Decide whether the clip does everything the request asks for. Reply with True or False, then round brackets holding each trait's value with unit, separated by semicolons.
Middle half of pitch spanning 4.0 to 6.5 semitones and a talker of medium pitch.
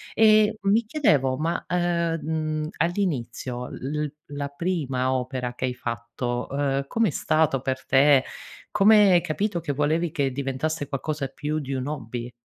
True (4.5 semitones; 145 Hz)